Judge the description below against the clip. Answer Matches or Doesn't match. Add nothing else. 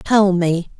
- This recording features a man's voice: Doesn't match